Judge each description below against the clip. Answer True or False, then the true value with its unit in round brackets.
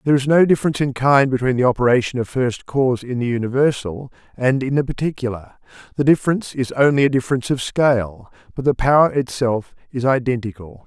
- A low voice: True (130 Hz)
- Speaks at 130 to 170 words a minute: False (180 wpm)